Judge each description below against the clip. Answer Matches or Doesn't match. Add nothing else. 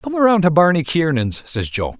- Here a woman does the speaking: Doesn't match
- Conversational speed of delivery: Doesn't match